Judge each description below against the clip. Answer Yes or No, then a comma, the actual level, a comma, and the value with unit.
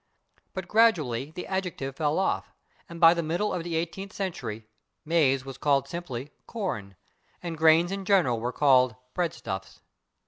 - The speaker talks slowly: No, average, 150 wpm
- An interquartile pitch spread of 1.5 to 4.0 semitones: No, average, 5.1 semitones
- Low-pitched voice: No, medium, 160 Hz